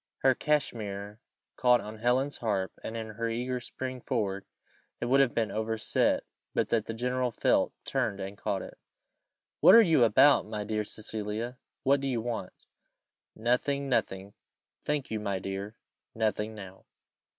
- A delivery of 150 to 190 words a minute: Yes, average, 155 wpm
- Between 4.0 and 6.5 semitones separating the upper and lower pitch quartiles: No, average, 3.3 semitones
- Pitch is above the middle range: No, low, 115 Hz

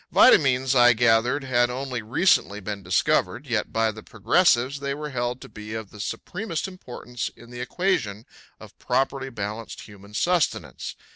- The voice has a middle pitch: No, low, 120 Hz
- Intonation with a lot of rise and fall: No, average, 4.0 semitones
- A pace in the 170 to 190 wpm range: No, average, 155 wpm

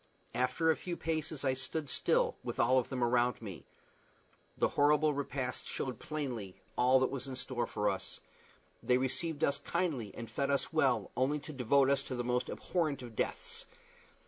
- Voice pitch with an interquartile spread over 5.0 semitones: No, average, 3.3 semitones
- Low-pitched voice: Yes, low, 130 Hz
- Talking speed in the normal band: Yes, average, 180 wpm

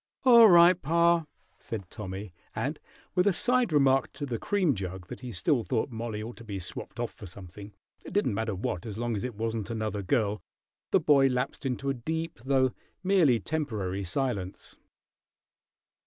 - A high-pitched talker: No, low, 120 Hz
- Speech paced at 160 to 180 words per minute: Yes, average, 175 wpm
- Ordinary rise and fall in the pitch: No, wide, 6.7 semitones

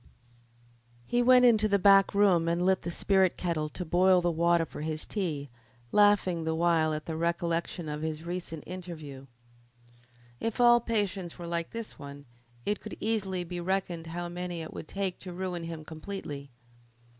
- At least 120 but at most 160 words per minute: No, average, 170 wpm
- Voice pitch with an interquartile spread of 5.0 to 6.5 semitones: No, average, 3.1 semitones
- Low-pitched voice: No, medium, 175 Hz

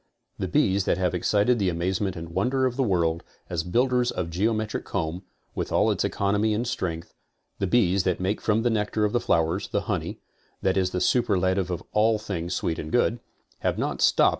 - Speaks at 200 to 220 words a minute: Yes, fast, 205 wpm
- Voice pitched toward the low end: Yes, very low, 95 Hz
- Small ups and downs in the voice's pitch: No, average, 3.8 semitones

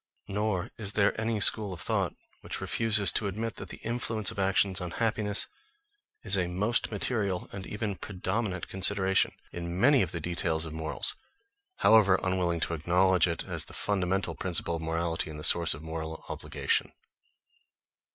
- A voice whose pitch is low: Yes, very low, 95 Hz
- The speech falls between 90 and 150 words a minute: No, average, 165 wpm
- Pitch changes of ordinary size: Yes, average, 3.4 semitones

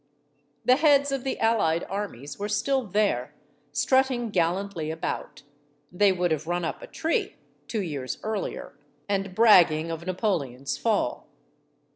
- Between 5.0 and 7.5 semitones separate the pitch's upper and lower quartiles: Yes, wide, 5.6 semitones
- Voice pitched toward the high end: Yes, high, 195 Hz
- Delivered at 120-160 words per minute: Yes, slow, 135 wpm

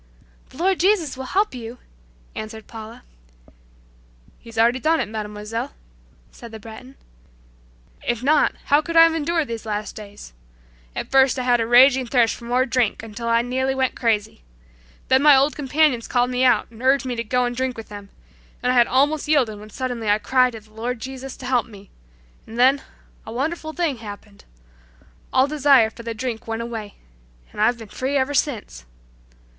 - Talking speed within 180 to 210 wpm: Yes, average, 185 wpm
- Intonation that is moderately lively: Yes, average, 3.1 semitones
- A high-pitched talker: Yes, high, 245 Hz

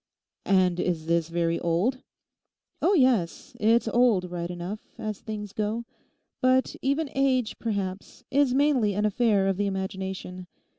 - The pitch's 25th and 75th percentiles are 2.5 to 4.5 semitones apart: No, average, 5.2 semitones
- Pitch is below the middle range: No, high, 205 Hz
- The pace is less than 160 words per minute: Yes, average, 140 wpm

